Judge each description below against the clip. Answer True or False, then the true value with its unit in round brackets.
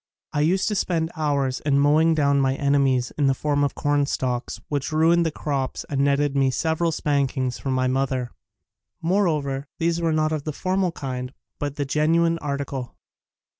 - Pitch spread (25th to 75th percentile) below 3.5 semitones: True (2.8 semitones)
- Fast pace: False (175 wpm)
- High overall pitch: False (145 Hz)